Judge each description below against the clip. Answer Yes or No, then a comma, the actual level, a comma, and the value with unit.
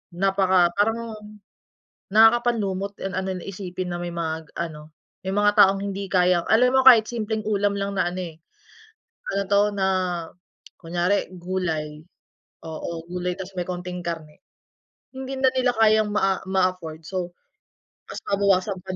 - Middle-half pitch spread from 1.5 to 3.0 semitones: Yes, narrow, 2.6 semitones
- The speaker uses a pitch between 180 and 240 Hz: Yes, high, 190 Hz